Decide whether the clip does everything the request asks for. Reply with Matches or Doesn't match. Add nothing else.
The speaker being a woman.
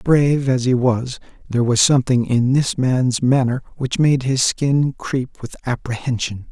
Doesn't match